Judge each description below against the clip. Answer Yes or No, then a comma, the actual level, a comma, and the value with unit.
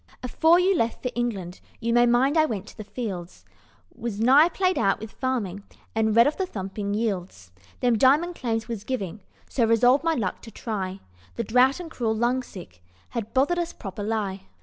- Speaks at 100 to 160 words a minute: No, average, 190 wpm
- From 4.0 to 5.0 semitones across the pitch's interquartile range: Yes, average, 4.3 semitones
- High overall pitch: Yes, high, 230 Hz